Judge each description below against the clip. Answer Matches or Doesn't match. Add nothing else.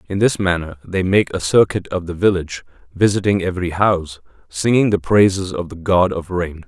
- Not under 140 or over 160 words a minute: Doesn't match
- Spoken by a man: Matches